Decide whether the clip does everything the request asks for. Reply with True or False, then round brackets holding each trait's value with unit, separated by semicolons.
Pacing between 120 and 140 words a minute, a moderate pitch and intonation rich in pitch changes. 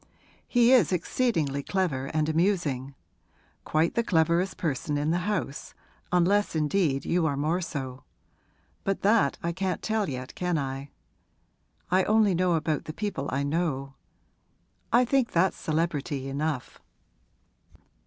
False (135 wpm; 165 Hz; 5.0 semitones)